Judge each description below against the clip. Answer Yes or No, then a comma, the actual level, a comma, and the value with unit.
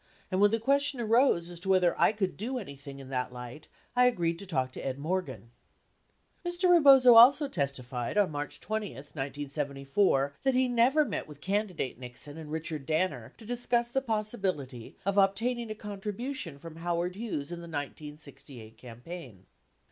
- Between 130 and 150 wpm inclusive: No, average, 170 wpm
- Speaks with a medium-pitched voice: Yes, medium, 175 Hz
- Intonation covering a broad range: Yes, wide, 8.3 semitones